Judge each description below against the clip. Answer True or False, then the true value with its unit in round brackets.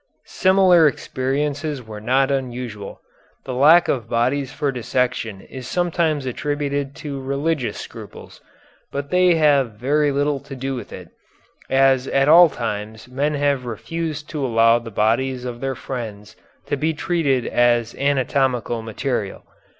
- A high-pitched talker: False (135 Hz)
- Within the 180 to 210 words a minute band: False (140 wpm)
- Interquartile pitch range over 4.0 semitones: False (3.3 semitones)